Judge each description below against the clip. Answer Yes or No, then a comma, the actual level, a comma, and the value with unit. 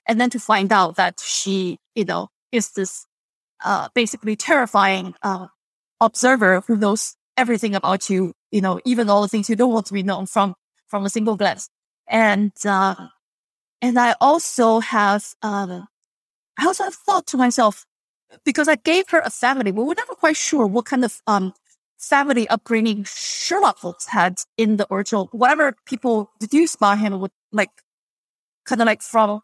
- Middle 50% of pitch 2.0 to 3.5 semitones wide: No, average, 3.9 semitones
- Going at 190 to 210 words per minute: No, average, 175 wpm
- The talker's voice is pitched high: Yes, high, 220 Hz